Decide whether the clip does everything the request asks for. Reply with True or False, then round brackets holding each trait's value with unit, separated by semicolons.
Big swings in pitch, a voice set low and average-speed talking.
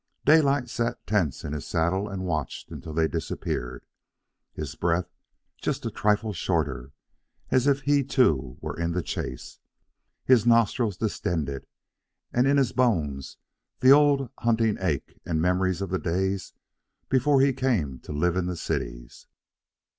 True (7.5 semitones; 95 Hz; 145 wpm)